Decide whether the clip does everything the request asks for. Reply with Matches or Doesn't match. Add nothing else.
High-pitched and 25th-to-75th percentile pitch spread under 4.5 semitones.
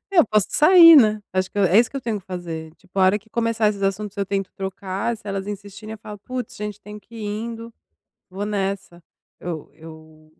Matches